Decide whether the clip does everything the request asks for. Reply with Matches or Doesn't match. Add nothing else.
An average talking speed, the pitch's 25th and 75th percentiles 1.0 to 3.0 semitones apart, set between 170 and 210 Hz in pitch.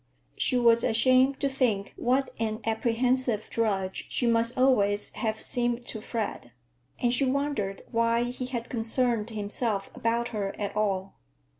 Doesn't match